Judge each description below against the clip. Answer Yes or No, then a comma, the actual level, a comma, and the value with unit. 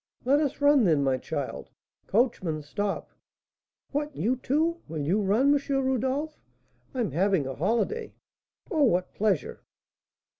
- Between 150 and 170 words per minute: No, slow, 135 wpm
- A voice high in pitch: Yes, high, 240 Hz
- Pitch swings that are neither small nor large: No, wide, 7.9 semitones